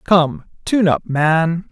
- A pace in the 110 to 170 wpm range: Yes, average, 140 wpm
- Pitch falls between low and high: Yes, medium, 170 Hz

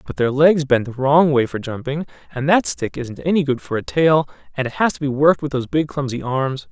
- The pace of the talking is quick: Yes, fast, 260 wpm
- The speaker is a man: Yes, male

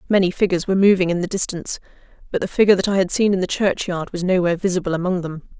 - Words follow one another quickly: Yes, fast, 235 wpm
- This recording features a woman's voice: Yes, female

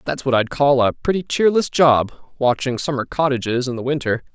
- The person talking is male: Yes, male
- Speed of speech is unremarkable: Yes, average, 180 wpm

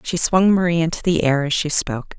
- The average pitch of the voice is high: No, medium, 165 Hz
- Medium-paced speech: No, fast, 245 wpm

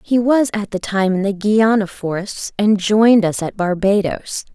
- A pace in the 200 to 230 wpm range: No, average, 185 wpm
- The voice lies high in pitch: Yes, high, 205 Hz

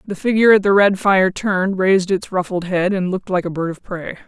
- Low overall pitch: No, high, 190 Hz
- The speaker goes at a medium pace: No, fast, 255 wpm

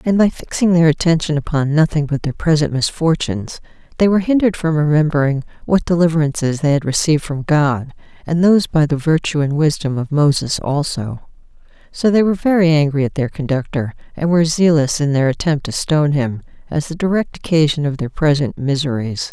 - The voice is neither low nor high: Yes, medium, 150 Hz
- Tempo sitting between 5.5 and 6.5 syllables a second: Yes, 5.7 syllables/s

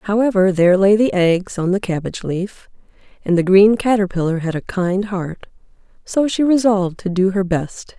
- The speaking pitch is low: No, high, 195 Hz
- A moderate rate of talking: Yes, average, 180 wpm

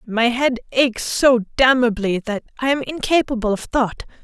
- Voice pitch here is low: No, high, 245 Hz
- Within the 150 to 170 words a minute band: Yes, average, 155 wpm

